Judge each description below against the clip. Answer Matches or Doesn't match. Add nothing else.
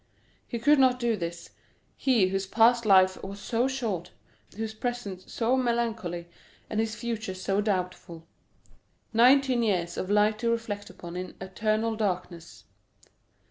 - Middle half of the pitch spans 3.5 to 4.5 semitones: Matches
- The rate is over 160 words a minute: Doesn't match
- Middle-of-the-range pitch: Doesn't match